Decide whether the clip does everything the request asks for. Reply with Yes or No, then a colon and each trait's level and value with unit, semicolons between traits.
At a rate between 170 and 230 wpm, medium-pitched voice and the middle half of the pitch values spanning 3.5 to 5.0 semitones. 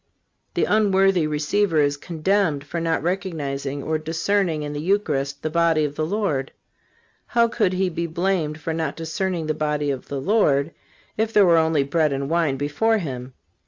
Yes: average, 175 wpm; medium, 160 Hz; average, 4.4 semitones